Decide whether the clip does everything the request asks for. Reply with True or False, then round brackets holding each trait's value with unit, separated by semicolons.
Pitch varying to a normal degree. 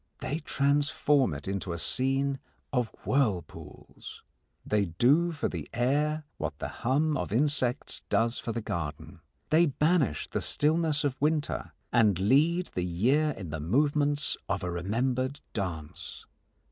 False (7.0 semitones)